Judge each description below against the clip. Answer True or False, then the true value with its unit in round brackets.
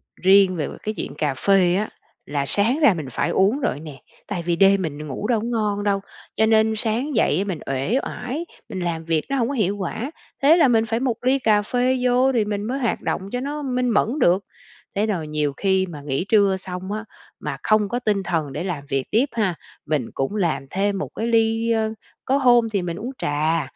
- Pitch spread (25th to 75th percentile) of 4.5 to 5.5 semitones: True (5.1 semitones)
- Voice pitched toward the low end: False (205 Hz)